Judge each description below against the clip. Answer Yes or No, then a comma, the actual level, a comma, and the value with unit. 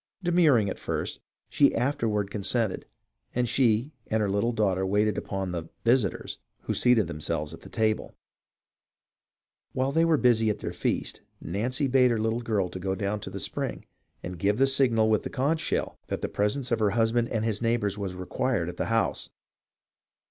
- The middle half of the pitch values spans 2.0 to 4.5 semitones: Yes, average, 3.8 semitones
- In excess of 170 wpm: Yes, average, 185 wpm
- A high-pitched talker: No, low, 110 Hz